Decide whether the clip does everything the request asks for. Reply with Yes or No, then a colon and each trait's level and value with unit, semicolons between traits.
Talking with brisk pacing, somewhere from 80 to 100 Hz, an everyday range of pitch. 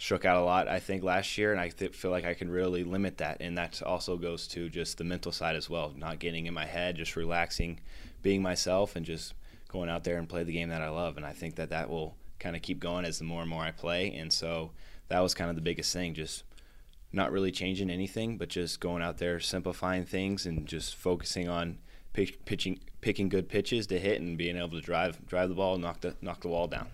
No: fast, 250 wpm; very low, 85 Hz; narrow, 1.8 semitones